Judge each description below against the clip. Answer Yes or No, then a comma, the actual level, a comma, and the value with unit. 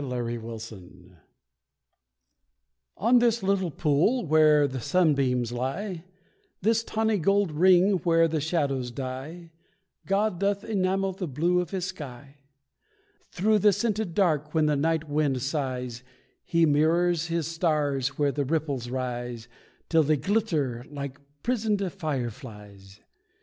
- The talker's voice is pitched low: No, medium, 155 Hz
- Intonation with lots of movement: Yes, wide, 6.0 semitones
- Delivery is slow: Yes, slow, 130 wpm